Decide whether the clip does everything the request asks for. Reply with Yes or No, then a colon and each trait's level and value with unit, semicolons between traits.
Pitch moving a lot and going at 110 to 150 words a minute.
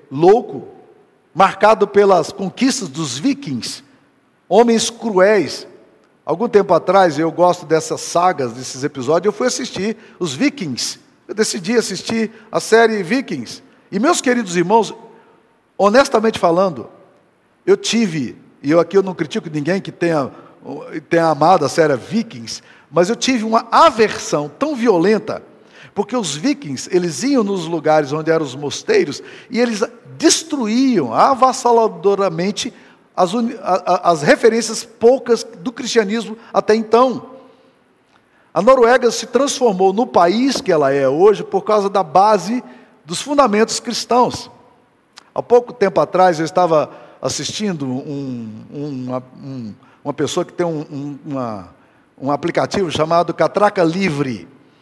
Yes: wide, 6.6 semitones; average, 135 wpm